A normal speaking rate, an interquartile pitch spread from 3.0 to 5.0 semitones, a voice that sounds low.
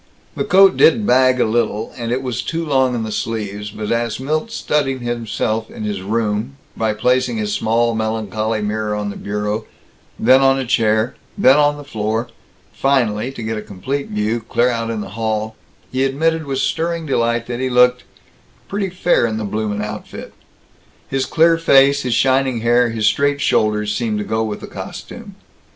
Yes: average, 185 wpm; average, 3.7 semitones; low, 115 Hz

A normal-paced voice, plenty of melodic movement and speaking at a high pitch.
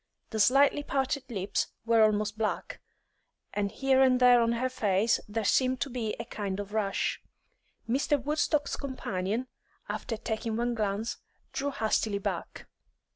No: average, 145 wpm; average, 3.6 semitones; high, 230 Hz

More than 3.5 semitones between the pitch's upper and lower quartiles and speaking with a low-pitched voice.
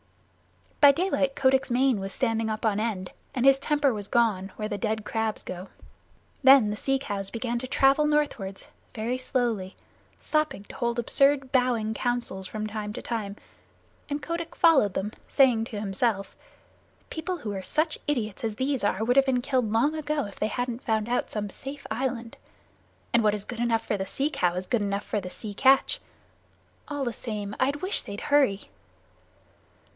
No: average, 4.5 semitones; high, 235 Hz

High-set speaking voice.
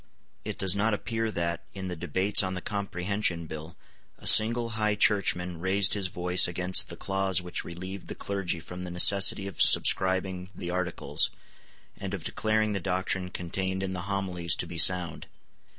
No: very low, 95 Hz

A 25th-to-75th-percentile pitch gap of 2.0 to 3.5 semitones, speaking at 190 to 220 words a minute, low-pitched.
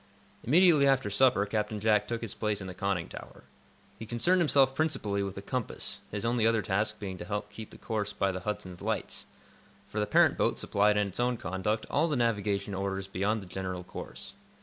Yes: average, 3.0 semitones; average, 200 wpm; low, 105 Hz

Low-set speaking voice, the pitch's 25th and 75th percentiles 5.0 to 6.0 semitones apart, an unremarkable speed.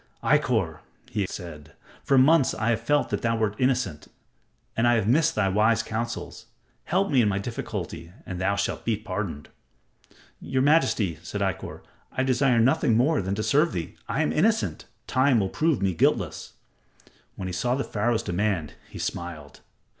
Yes: low, 115 Hz; wide, 5.4 semitones; average, 170 wpm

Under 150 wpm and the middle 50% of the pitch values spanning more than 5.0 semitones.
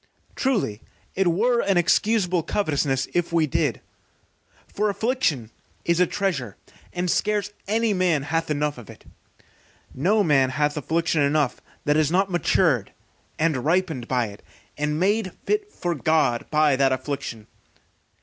Yes: average, 140 wpm; wide, 5.4 semitones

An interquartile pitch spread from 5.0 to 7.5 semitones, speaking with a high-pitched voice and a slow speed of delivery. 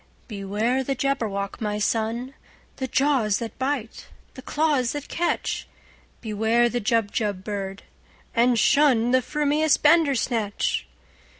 No: average, 4.3 semitones; high, 240 Hz; slow, 100 wpm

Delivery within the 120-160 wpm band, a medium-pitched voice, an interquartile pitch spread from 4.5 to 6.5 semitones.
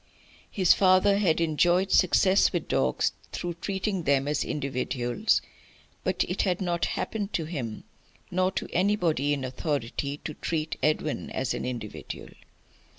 Yes: average, 140 wpm; medium, 165 Hz; average, 5.0 semitones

